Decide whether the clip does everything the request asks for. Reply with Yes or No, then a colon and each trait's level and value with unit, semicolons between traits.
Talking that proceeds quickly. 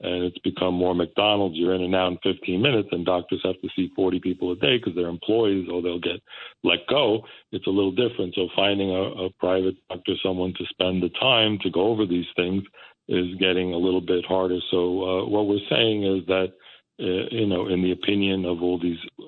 Yes: fast, 220 wpm